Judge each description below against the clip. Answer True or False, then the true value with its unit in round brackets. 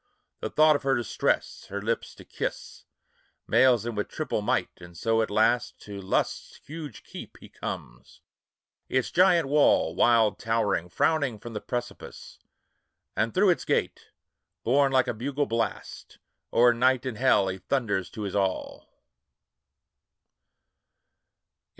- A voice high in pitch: False (120 Hz)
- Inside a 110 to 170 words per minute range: True (140 wpm)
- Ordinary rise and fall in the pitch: True (4.4 semitones)